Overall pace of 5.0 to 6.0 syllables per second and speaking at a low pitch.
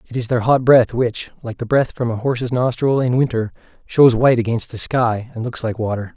Yes: 5.4 syllables/s; low, 120 Hz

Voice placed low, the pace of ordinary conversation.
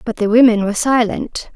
No: high, 225 Hz; average, 195 wpm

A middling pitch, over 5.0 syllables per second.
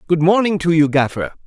Yes: medium, 165 Hz; 6.0 syllables/s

